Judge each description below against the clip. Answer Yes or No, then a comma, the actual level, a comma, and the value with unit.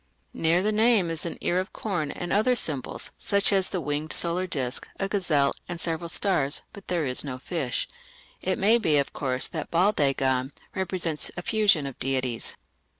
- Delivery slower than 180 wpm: No, average, 185 wpm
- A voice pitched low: No, medium, 170 Hz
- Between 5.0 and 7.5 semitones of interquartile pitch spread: Yes, wide, 5.4 semitones